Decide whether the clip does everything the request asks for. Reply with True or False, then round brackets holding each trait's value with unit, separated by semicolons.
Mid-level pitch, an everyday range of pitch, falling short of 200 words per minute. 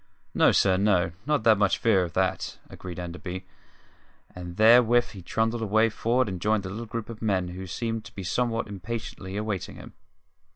False (105 Hz; 3.4 semitones; 175 wpm)